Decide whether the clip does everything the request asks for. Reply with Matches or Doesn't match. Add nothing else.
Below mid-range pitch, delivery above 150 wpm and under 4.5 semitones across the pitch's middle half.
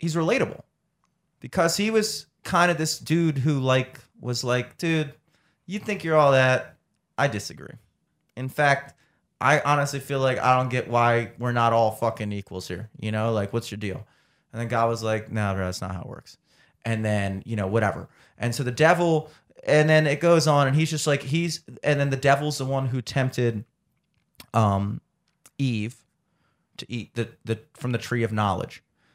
Doesn't match